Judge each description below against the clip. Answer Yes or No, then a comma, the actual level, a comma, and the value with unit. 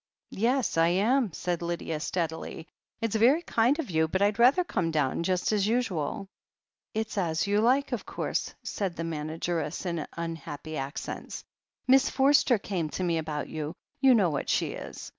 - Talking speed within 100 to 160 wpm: No, average, 175 wpm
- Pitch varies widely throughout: Yes, wide, 6.1 semitones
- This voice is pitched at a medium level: Yes, medium, 180 Hz